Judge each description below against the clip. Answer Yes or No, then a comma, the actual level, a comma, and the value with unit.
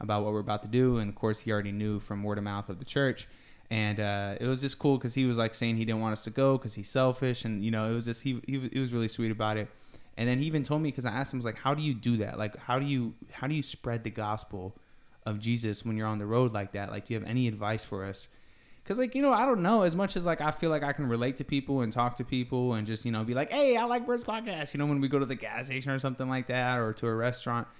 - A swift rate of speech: Yes, fast, 320 wpm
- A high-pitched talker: No, low, 120 Hz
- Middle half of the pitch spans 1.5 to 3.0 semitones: No, average, 3.9 semitones